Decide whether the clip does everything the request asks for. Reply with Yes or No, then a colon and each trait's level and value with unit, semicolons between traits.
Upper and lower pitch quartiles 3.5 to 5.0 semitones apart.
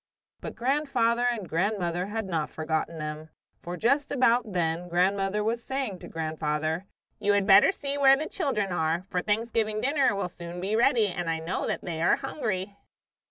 No: wide, 5.4 semitones